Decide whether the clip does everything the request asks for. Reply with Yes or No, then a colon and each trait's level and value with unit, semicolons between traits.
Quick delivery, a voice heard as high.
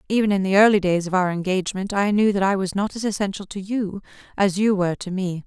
Yes: fast, 250 wpm; high, 195 Hz